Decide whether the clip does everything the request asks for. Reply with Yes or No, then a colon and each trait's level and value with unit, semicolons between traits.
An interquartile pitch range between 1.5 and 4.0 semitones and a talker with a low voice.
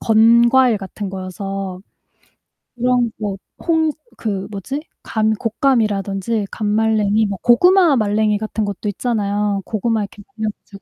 No: average, 2.7 semitones; high, 215 Hz